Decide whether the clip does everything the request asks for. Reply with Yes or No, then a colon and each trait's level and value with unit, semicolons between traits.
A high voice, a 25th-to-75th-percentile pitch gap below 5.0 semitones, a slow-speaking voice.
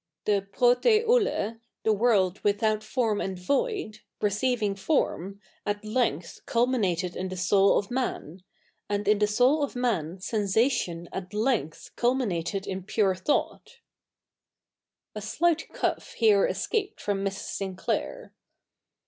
Yes: high, 210 Hz; average, 4.3 semitones; slow, 125 wpm